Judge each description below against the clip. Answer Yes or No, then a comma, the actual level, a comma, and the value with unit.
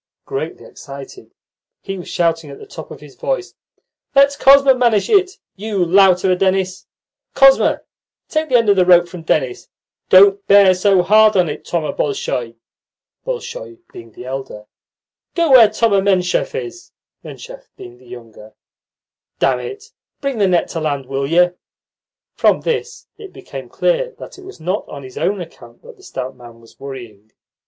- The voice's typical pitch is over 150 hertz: Yes, medium, 185 Hz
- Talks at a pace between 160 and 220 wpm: No, average, 150 wpm